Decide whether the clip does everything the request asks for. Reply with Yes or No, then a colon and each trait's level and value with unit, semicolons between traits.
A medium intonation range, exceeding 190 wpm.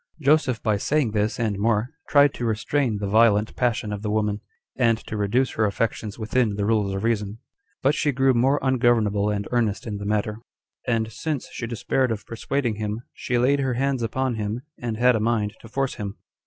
Yes: average, 3.2 semitones; fast, 205 wpm